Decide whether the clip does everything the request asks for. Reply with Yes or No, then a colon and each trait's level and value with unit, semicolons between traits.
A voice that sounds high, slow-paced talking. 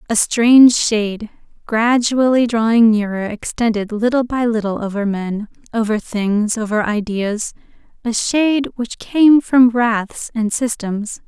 Yes: high, 225 Hz; slow, 130 wpm